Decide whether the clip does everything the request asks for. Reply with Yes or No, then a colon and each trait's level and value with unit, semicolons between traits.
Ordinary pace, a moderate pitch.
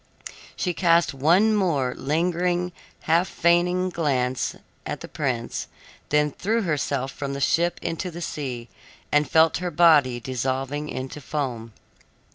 No: slow, 130 wpm; medium, 150 Hz